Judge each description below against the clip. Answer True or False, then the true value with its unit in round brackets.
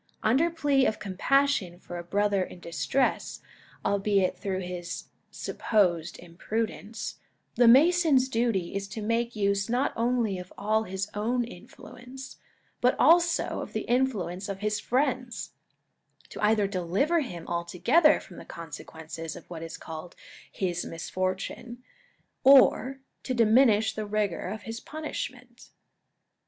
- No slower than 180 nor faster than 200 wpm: False (140 wpm)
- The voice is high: True (215 Hz)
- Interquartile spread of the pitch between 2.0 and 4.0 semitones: False (5.3 semitones)